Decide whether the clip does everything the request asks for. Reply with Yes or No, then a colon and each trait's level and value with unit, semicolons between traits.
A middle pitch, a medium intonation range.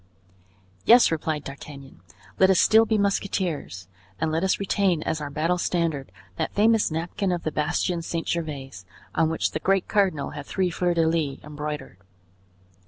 Yes: medium, 165 Hz; average, 4.0 semitones